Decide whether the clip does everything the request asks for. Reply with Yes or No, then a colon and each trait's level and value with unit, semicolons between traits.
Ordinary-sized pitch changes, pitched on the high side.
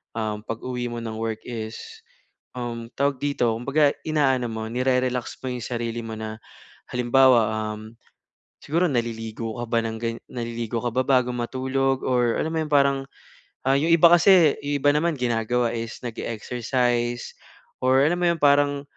No: average, 3.3 semitones; low, 125 Hz